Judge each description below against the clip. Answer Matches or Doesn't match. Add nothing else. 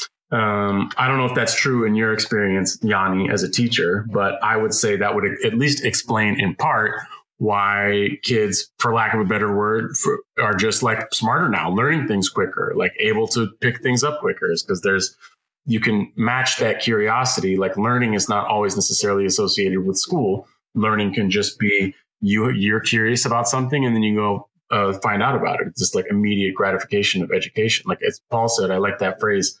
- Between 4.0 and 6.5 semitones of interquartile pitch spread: Doesn't match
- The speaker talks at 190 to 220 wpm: Matches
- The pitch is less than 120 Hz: Matches